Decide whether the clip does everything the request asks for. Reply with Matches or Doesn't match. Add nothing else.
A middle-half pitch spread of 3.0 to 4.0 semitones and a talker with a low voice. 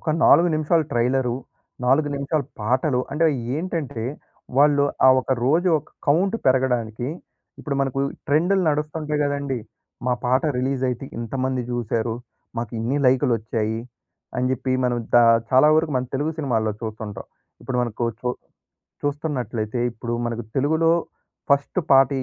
Matches